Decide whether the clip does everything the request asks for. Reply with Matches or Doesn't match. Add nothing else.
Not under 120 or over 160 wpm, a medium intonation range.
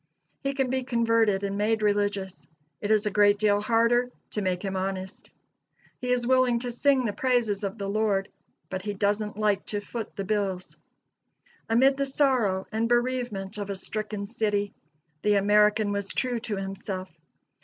Doesn't match